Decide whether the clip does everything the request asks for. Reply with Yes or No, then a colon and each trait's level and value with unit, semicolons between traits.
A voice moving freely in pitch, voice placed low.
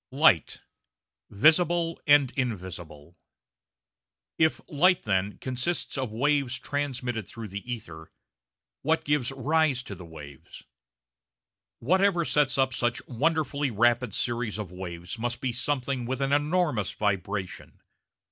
Yes: wide, 6.0 semitones; low, 125 Hz